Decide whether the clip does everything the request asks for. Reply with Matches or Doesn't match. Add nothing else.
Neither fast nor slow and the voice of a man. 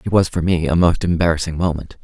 Doesn't match